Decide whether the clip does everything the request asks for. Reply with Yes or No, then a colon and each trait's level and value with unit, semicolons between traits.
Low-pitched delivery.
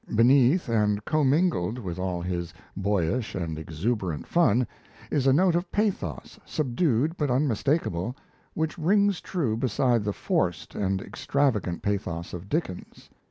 Yes: low, 120 Hz